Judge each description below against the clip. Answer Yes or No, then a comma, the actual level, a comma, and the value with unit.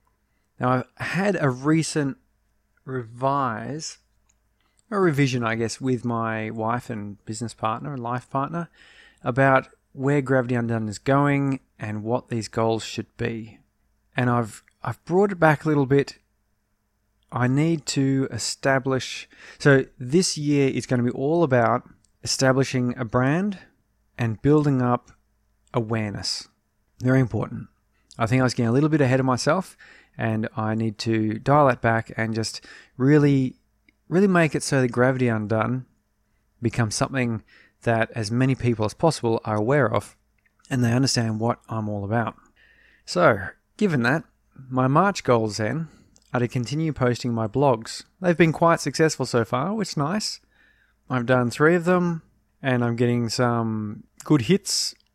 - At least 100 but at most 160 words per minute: Yes, average, 155 wpm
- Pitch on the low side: Yes, low, 125 Hz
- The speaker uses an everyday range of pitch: Yes, average, 3.9 semitones